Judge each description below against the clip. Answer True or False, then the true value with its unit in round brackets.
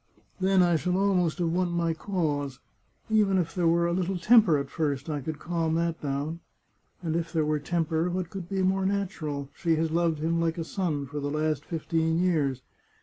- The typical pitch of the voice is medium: True (165 Hz)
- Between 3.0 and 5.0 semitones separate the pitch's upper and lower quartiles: False (2.6 semitones)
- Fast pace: True (210 wpm)